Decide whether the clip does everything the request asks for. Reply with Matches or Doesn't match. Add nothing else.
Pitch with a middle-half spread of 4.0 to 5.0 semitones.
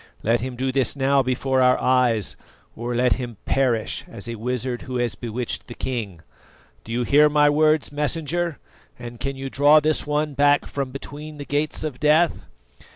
Doesn't match